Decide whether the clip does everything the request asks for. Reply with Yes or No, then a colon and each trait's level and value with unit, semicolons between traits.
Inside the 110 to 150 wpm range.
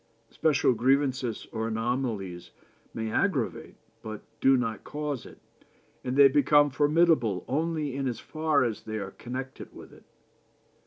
Yes: average, 140 wpm